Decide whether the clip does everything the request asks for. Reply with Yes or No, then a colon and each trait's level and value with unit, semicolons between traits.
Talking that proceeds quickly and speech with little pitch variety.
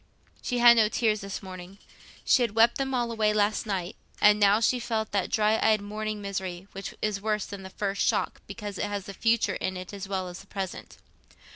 Yes: fast, 220 wpm; narrow, 2.0 semitones